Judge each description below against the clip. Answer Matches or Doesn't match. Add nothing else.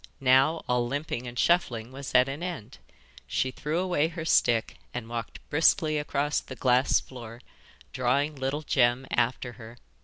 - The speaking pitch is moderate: Doesn't match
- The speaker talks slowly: Doesn't match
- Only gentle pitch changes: Doesn't match